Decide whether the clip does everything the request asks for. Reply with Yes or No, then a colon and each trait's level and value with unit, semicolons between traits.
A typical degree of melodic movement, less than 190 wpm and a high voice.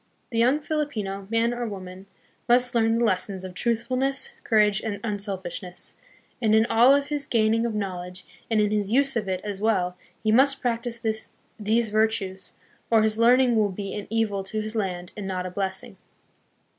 Yes: average, 3.2 semitones; average, 180 wpm; high, 215 Hz